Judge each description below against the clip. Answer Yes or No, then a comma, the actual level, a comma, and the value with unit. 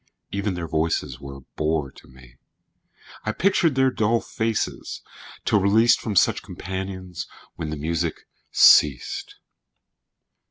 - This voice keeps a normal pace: No, slow, 125 wpm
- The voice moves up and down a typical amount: No, wide, 5.9 semitones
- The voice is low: Yes, very low, 90 Hz